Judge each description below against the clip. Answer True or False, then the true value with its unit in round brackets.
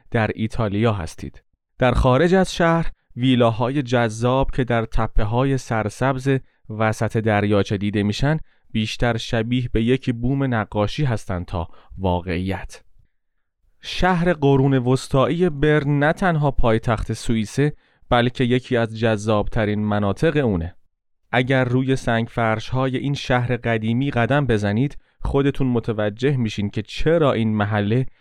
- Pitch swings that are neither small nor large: True (3.8 semitones)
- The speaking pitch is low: True (120 Hz)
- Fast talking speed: False (125 wpm)